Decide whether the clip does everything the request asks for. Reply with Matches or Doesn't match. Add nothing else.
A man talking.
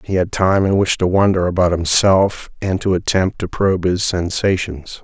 Matches